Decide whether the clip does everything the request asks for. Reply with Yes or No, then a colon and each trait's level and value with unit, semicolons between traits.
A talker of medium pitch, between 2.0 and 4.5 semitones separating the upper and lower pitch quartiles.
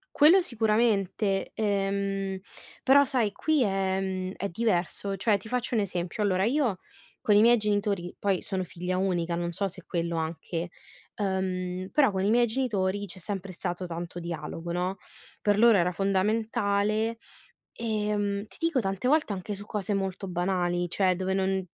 No: high, 195 Hz; average, 2.7 semitones